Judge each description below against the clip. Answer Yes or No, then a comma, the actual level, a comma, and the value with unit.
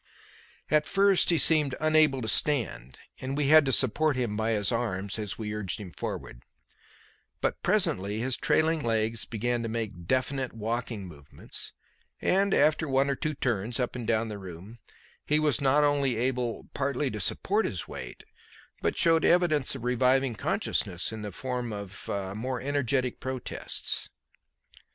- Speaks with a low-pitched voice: Yes, low, 125 Hz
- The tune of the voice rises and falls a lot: No, average, 4.7 semitones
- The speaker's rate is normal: Yes, average, 150 wpm